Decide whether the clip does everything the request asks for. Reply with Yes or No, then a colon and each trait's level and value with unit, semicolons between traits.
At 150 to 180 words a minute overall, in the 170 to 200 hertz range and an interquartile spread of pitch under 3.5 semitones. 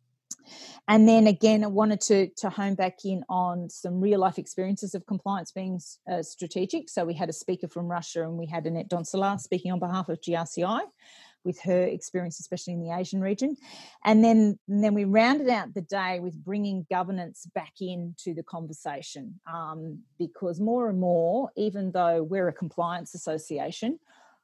Yes: average, 175 wpm; medium, 185 Hz; average, 2.9 semitones